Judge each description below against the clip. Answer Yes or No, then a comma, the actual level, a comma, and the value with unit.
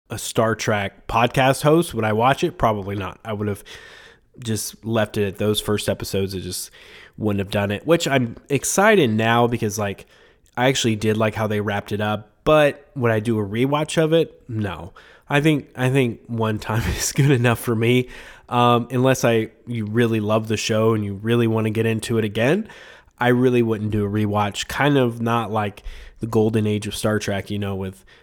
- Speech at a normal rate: No, fast, 210 wpm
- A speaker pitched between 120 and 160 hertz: No, low, 110 Hz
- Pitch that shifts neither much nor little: Yes, average, 3.0 semitones